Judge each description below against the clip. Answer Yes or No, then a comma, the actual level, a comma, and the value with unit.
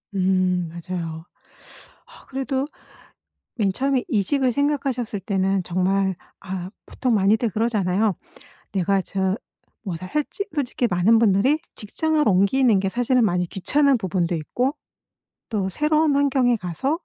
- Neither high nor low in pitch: No, high, 210 Hz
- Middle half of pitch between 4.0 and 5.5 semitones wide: No, wide, 5.9 semitones